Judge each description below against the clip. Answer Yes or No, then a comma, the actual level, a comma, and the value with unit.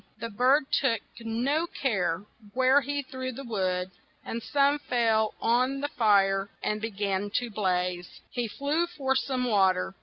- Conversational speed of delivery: Yes, average, 160 wpm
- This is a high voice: Yes, high, 230 Hz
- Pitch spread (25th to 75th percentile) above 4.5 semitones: Yes, average, 5.2 semitones